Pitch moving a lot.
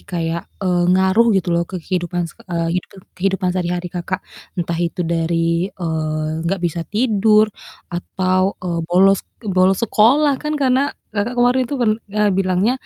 No: average, 3.6 semitones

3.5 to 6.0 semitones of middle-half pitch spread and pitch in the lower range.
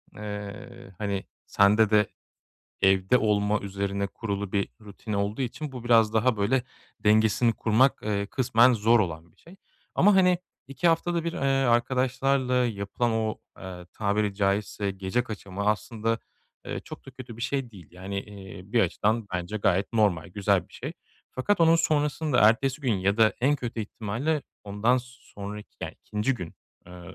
Yes: average, 3.9 semitones; low, 110 Hz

